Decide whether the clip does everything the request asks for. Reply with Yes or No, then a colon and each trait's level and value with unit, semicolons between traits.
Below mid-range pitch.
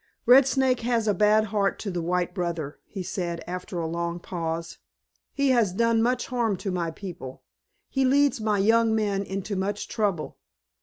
No: high, 200 Hz